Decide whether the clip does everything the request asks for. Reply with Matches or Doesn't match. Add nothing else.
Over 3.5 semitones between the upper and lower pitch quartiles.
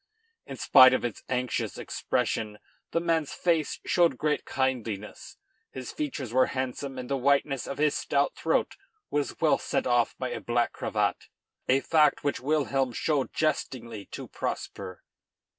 Doesn't match